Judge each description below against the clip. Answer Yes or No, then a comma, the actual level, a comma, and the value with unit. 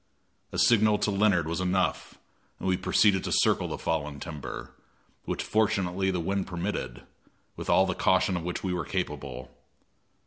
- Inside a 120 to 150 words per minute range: No, average, 165 wpm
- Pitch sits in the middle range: No, very low, 90 Hz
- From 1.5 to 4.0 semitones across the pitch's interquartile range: Yes, average, 2.9 semitones